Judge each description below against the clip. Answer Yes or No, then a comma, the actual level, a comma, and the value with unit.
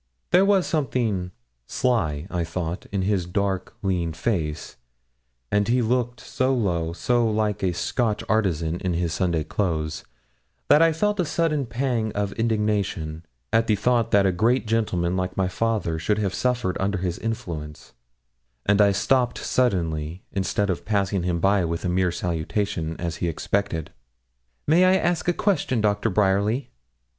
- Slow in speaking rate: No, average, 160 wpm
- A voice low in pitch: Yes, low, 100 Hz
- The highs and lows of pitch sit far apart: No, average, 5.0 semitones